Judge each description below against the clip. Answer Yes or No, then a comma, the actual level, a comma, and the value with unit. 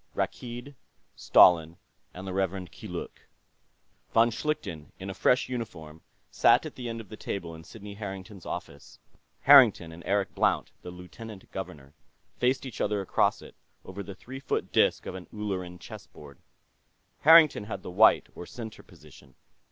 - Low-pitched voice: Yes, very low, 95 Hz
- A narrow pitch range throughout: No, average, 4.4 semitones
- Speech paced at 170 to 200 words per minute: No, average, 160 wpm